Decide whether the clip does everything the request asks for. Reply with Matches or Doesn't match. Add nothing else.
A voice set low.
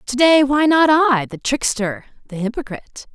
Doesn't match